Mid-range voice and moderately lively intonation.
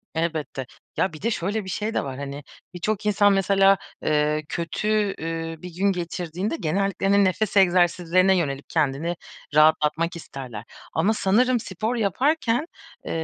Yes: medium, 180 Hz; average, 4.1 semitones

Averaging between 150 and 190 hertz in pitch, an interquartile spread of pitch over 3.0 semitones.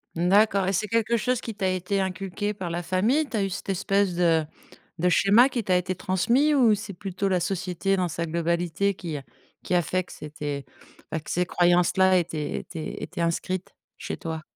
No: medium, 185 Hz; narrow, 2.6 semitones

